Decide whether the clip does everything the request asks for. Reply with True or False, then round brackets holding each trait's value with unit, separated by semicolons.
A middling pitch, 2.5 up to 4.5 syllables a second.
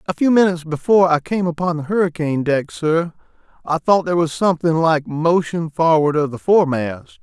False (160 Hz; 5.8 syllables/s)